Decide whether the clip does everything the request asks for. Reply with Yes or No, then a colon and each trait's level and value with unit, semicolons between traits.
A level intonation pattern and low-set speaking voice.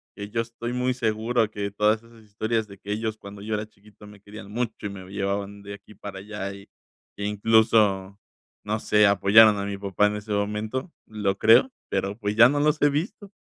Yes: narrow, 1.7 semitones; low, 105 Hz